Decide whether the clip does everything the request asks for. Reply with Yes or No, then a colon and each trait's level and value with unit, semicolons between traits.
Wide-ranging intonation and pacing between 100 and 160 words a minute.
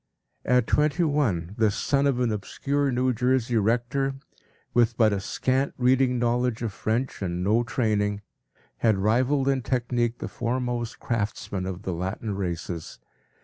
No: average, 3.8 semitones; average, 150 wpm